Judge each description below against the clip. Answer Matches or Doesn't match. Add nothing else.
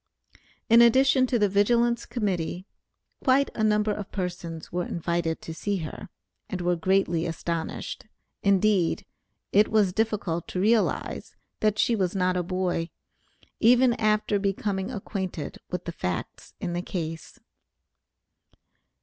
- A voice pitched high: Matches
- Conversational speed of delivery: Doesn't match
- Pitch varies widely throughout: Doesn't match